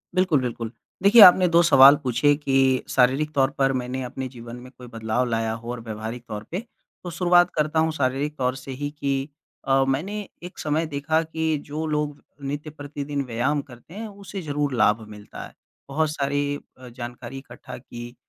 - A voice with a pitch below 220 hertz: Yes, medium, 140 Hz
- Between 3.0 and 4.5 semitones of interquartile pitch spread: Yes, average, 3.6 semitones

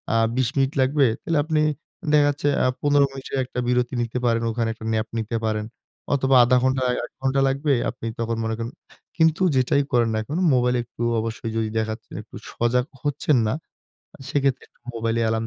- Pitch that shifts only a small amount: No, average, 3.2 semitones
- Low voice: Yes, low, 125 Hz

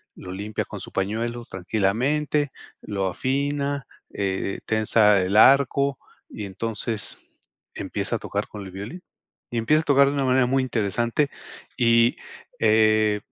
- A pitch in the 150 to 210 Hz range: No, low, 115 Hz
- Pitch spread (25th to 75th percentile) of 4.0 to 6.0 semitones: Yes, average, 4.8 semitones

